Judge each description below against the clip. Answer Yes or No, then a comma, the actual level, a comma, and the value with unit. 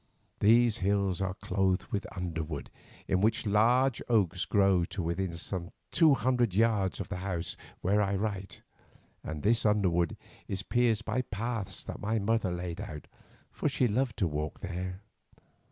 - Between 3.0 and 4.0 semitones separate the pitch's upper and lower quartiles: Yes, average, 3.6 semitones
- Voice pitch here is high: No, low, 100 Hz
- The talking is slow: No, average, 155 wpm